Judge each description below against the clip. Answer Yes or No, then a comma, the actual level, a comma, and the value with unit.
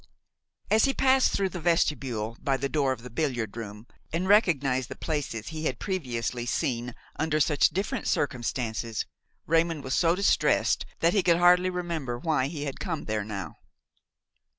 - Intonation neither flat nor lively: No, wide, 6.1 semitones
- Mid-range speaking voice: Yes, medium, 145 Hz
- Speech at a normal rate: Yes, average, 165 wpm